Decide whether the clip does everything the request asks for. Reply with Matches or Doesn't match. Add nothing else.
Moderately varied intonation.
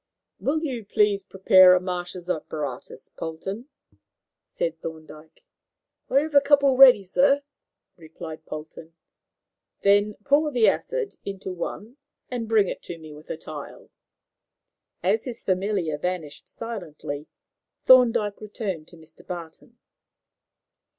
Doesn't match